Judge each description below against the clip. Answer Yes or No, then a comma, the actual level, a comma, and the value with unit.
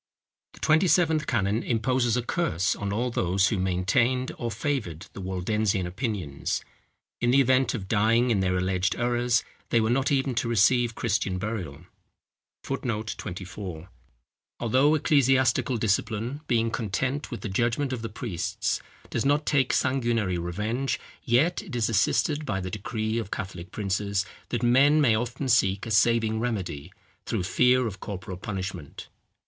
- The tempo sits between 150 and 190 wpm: Yes, average, 155 wpm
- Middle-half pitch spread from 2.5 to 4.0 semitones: No, average, 4.8 semitones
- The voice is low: Yes, low, 115 Hz